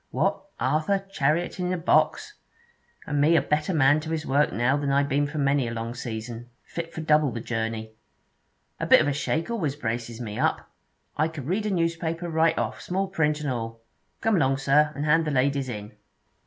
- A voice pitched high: No, medium, 145 Hz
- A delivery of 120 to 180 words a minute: No, average, 200 wpm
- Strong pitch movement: No, average, 4.3 semitones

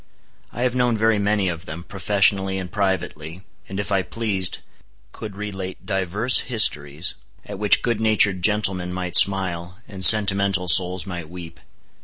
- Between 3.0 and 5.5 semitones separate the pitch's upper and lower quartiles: No, narrow, 2.6 semitones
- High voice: No, very low, 95 Hz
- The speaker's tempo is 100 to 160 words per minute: Yes, average, 150 wpm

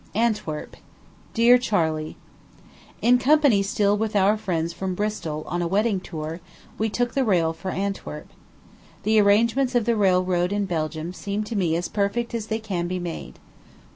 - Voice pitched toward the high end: Yes, high, 200 Hz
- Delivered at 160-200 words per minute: Yes, average, 165 wpm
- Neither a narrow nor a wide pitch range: Yes, average, 4.2 semitones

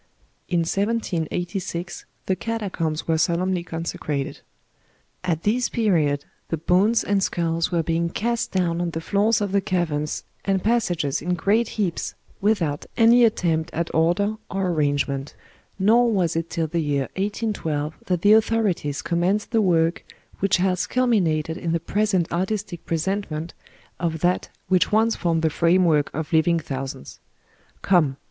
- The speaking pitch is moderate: Yes, medium, 175 Hz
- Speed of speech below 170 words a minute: Yes, average, 150 wpm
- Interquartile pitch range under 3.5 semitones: No, average, 3.8 semitones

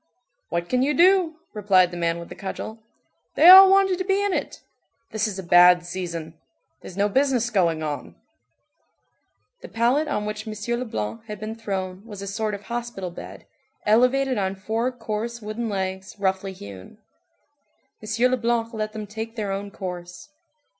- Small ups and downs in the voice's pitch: No, average, 4.1 semitones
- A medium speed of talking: Yes, average, 165 wpm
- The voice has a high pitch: Yes, high, 215 Hz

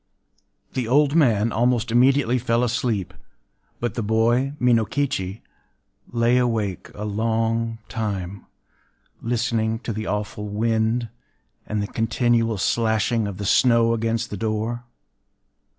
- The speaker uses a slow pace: Yes, slow, 120 wpm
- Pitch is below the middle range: Yes, low, 115 Hz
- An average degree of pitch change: No, narrow, 1.9 semitones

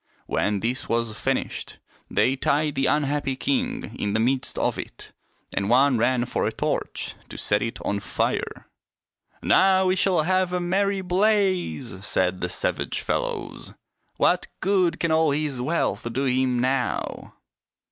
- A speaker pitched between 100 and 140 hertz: Yes, low, 135 Hz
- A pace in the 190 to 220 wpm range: No, average, 155 wpm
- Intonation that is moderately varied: No, wide, 7.6 semitones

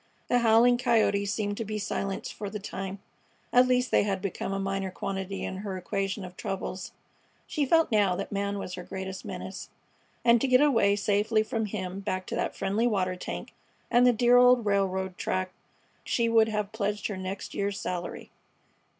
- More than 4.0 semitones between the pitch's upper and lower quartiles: No, average, 2.9 semitones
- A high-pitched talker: Yes, high, 200 Hz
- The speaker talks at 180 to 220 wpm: Yes, average, 185 wpm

